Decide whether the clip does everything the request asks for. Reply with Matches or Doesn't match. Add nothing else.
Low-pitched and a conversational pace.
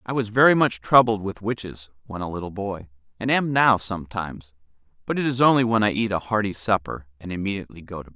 Doesn't match